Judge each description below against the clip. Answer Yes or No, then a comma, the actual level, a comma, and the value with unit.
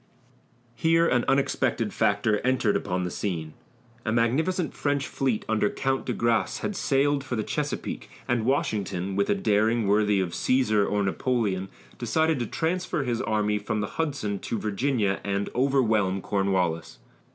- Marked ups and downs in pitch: No, average, 5.0 semitones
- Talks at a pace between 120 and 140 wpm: No, average, 150 wpm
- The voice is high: No, low, 110 Hz